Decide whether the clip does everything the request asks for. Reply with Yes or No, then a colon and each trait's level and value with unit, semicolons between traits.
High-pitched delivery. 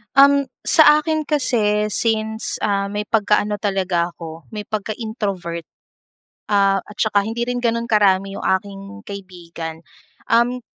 Yes: high, 210 Hz